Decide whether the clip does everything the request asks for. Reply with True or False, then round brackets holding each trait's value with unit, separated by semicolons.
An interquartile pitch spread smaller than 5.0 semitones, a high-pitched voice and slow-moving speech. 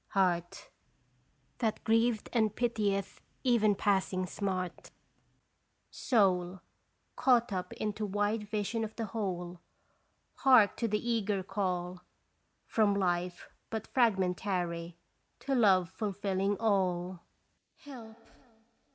True (3.2 semitones; 200 Hz; 100 wpm)